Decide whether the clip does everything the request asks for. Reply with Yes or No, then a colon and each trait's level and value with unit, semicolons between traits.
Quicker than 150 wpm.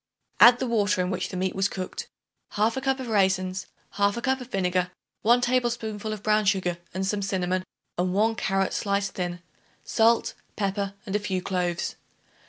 Yes: average, 175 wpm